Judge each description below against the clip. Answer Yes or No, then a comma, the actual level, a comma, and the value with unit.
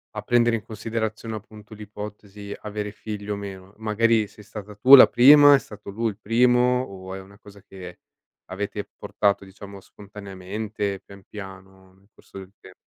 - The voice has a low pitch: Yes, low, 105 Hz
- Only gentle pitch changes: Yes, narrow, 2.0 semitones